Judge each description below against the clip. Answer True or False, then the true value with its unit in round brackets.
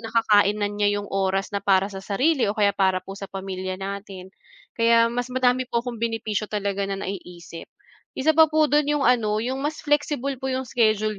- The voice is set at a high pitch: True (215 Hz)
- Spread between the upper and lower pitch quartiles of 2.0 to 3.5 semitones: False (4.5 semitones)